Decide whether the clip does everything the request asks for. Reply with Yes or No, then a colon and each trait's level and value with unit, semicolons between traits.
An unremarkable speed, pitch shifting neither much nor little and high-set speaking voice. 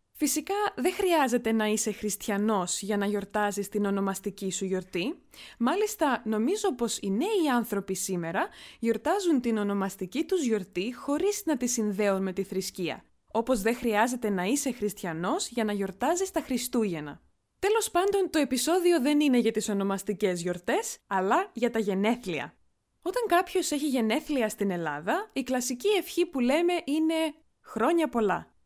No: average, 150 wpm; wide, 7.8 semitones; high, 235 Hz